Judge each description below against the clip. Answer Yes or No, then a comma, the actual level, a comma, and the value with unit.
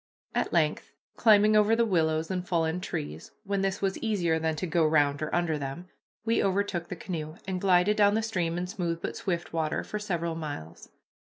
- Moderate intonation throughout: Yes, average, 3.7 semitones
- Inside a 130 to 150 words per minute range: No, average, 200 wpm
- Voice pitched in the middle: Yes, medium, 175 Hz